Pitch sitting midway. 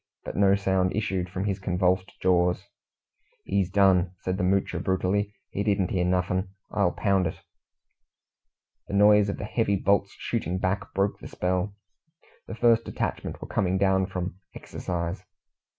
No: very low, 95 Hz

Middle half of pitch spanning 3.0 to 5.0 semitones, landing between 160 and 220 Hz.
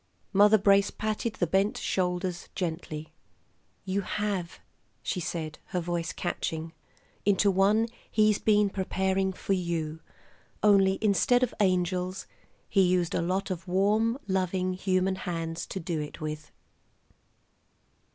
No: narrow, 2.5 semitones; medium, 185 Hz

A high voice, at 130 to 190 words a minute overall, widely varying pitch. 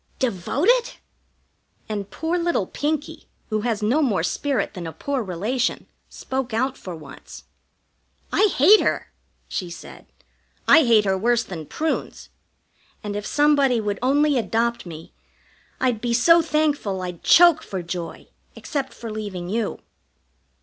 Yes: high, 235 Hz; average, 140 wpm; wide, 6.7 semitones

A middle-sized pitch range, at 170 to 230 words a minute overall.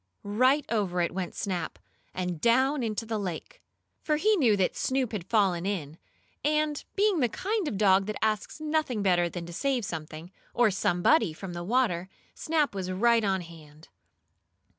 No: wide, 6.6 semitones; average, 175 wpm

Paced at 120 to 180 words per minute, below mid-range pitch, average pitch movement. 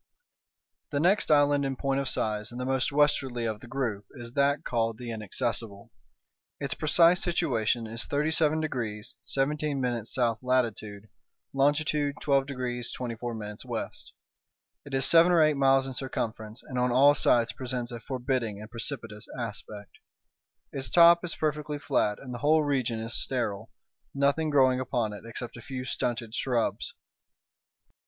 Yes: average, 150 wpm; low, 130 Hz; average, 3.7 semitones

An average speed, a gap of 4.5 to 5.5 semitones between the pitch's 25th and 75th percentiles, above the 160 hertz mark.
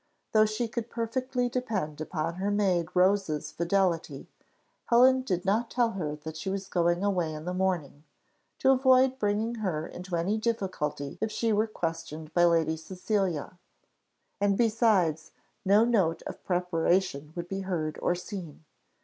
Yes: average, 150 wpm; average, 4.8 semitones; high, 190 Hz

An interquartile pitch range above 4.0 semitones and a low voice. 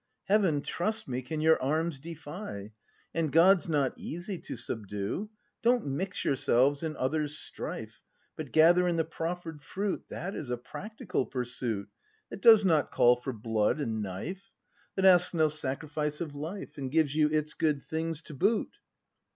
No: average, 4.7 semitones; medium, 155 Hz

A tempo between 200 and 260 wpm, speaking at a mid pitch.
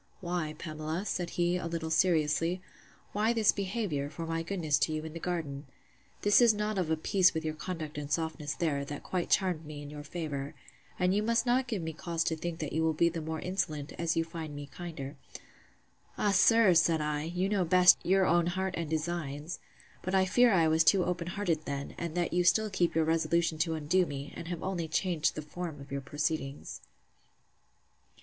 Yes: fast, 205 wpm; medium, 165 Hz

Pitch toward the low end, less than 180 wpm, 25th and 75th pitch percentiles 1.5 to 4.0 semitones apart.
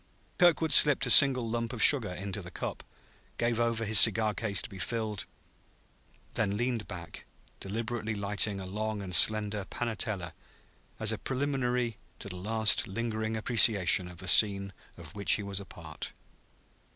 Yes: low, 110 Hz; average, 160 wpm; average, 2.9 semitones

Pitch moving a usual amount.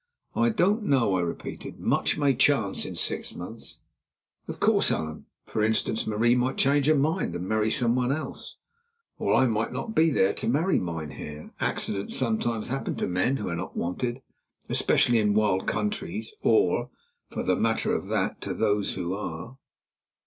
No: wide, 5.9 semitones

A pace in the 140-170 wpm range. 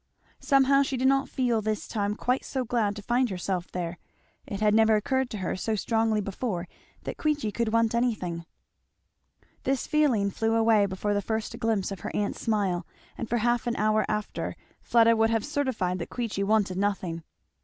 No: average, 185 wpm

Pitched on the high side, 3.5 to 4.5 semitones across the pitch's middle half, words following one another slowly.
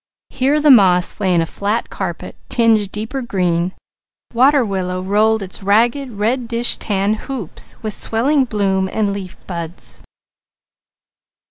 Yes: high, 210 Hz; average, 3.9 semitones; slow, 130 wpm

